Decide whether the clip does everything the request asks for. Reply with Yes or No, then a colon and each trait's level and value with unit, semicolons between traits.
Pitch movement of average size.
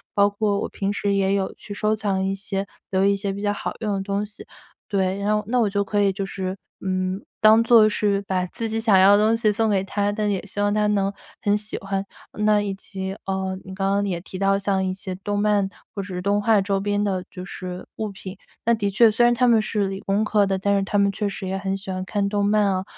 No: narrow, 1.4 semitones